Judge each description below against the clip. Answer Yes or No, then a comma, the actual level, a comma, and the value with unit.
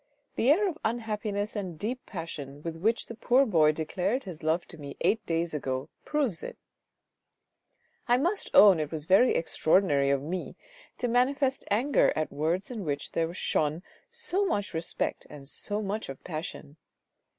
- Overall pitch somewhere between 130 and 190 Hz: Yes, medium, 185 Hz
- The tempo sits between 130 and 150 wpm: No, average, 170 wpm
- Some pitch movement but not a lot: No, wide, 7.2 semitones